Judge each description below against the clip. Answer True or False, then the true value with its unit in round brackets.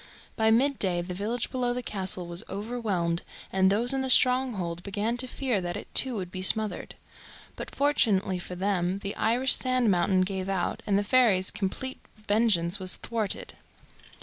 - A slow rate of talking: False (175 wpm)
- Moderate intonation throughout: True (4.7 semitones)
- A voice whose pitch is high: True (205 Hz)